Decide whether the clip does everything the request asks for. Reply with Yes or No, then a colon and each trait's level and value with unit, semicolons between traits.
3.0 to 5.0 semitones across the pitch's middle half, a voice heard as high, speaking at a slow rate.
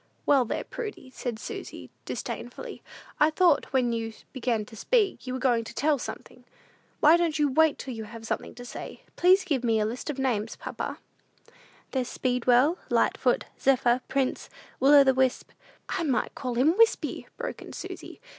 No: average, 3.9 semitones; very high, 260 Hz; average, 180 wpm